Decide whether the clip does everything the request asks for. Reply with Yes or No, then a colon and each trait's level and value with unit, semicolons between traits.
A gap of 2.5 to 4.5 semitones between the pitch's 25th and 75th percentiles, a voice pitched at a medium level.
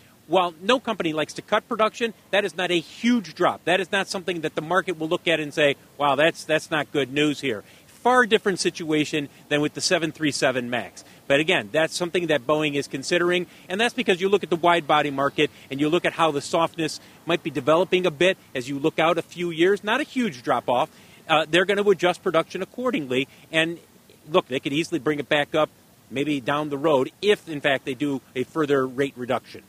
Yes: average, 4.0 semitones; medium, 160 Hz